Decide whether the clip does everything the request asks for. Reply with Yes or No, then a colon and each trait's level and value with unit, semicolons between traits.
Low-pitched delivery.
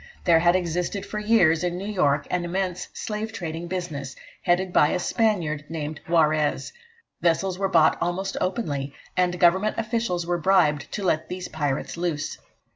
No: medium, 175 Hz